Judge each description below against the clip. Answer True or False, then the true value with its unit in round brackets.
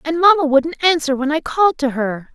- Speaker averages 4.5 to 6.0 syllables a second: True (5.6 syllables/s)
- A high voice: True (295 Hz)